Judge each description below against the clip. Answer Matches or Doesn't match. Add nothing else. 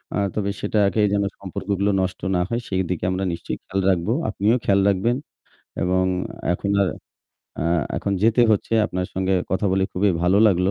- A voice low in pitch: Matches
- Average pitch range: Doesn't match